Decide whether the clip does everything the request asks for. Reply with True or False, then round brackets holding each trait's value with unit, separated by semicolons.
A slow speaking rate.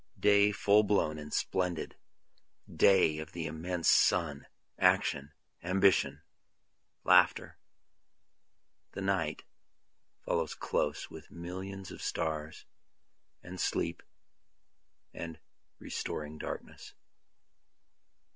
True (85 wpm)